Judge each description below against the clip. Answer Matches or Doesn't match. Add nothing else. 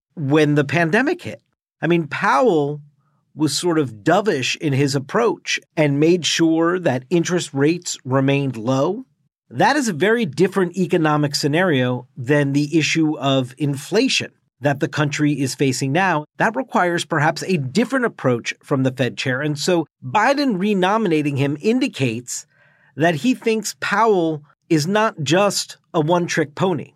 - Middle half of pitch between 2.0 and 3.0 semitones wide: Doesn't match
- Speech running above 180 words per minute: Doesn't match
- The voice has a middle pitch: Matches